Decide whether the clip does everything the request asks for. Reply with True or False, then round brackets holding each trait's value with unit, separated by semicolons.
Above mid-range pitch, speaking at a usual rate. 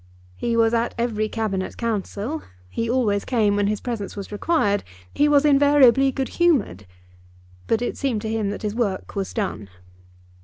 True (225 Hz; 165 wpm)